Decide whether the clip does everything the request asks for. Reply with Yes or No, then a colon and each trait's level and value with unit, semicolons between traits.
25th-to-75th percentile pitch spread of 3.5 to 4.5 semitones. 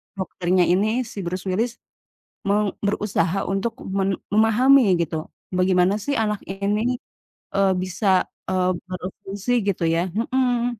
No: average, 2.9 semitones